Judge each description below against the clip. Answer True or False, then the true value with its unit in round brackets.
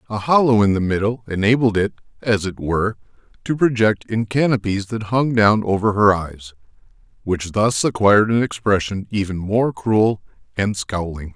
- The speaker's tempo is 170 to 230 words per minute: False (160 wpm)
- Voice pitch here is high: False (105 Hz)